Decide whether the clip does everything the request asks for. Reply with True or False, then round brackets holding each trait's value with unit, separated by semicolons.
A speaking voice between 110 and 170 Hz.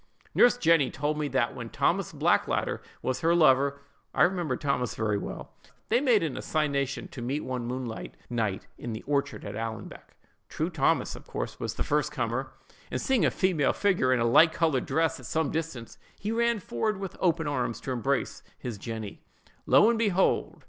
True (140 Hz)